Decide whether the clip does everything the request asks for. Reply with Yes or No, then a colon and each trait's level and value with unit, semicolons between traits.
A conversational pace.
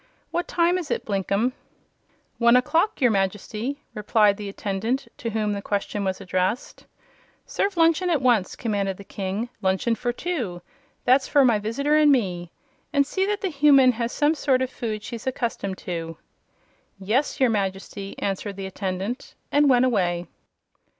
Yes: average, 160 wpm